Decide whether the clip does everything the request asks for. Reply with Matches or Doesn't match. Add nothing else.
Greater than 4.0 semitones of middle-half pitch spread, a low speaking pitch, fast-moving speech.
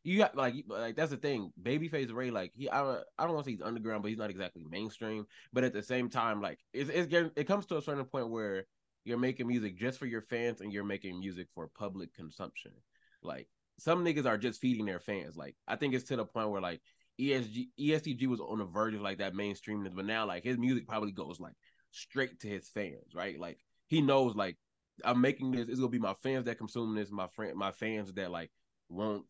Matches